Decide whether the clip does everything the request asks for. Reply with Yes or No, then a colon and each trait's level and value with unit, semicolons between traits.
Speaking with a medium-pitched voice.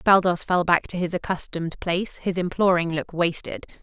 Yes: medium, 175 Hz